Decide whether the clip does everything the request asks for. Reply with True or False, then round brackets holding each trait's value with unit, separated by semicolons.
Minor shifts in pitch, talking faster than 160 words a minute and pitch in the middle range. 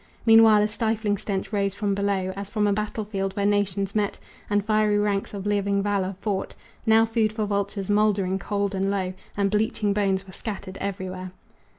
False (1.4 semitones; 185 wpm; 200 Hz)